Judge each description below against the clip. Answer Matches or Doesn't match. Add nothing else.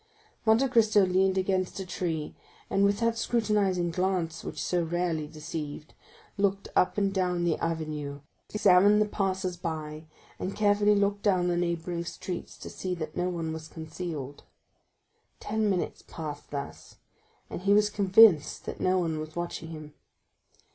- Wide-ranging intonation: Doesn't match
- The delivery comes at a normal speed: Matches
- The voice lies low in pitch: Doesn't match